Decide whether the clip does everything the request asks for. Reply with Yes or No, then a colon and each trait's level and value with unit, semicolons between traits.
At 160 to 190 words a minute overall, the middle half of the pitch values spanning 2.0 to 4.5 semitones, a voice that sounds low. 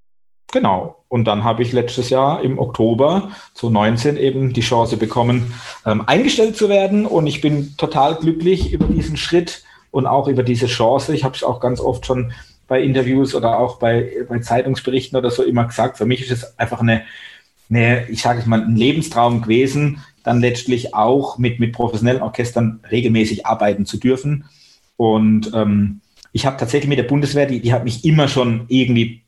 Yes: average, 185 wpm; average, 2.8 semitones; low, 125 Hz